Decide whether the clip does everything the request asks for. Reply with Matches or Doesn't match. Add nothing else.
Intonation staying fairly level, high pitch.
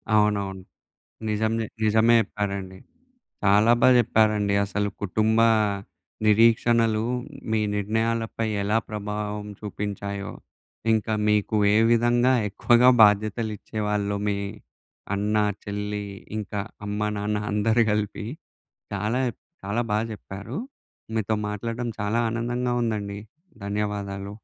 Doesn't match